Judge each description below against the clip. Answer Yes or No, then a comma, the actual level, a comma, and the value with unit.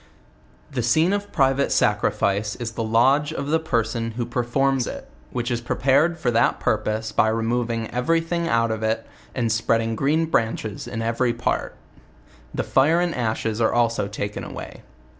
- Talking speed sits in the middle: Yes, average, 170 wpm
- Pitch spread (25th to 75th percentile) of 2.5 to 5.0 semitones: Yes, average, 3.5 semitones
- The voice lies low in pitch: Yes, low, 120 Hz